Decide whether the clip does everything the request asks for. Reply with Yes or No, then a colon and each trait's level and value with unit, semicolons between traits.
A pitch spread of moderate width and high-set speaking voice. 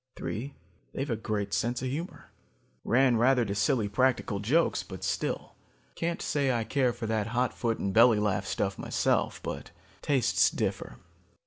No: average, 3.7 semitones; low, 120 Hz